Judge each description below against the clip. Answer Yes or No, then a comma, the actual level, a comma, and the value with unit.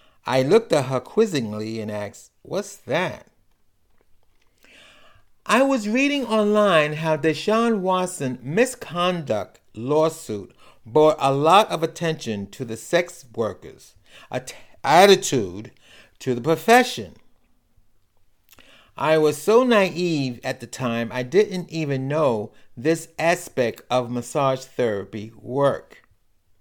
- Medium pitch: Yes, medium, 150 Hz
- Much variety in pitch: Yes, wide, 6.8 semitones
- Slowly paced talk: Yes, slow, 115 wpm